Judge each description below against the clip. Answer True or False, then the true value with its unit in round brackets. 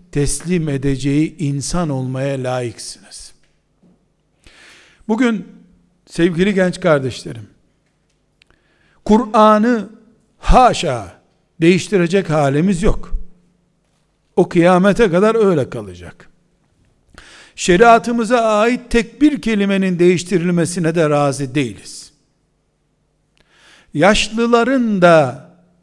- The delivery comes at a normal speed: False (70 wpm)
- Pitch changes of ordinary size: False (7.0 semitones)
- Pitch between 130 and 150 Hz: False (180 Hz)